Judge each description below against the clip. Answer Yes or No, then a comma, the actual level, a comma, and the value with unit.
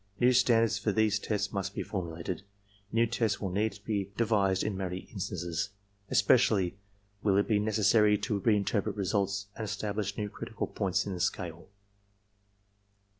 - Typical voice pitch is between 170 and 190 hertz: No, low, 100 Hz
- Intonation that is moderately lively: No, narrow, 2.1 semitones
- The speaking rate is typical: Yes, average, 160 wpm